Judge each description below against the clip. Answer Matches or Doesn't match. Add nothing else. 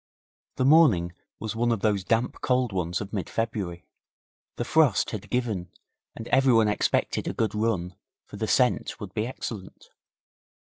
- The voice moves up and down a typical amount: Matches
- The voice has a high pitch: Doesn't match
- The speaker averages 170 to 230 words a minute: Doesn't match